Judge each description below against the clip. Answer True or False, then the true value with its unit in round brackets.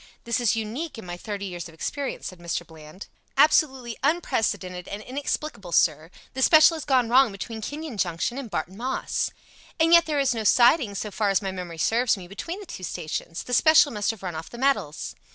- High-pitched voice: True (225 Hz)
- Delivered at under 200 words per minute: False (205 wpm)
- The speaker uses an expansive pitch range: True (6.9 semitones)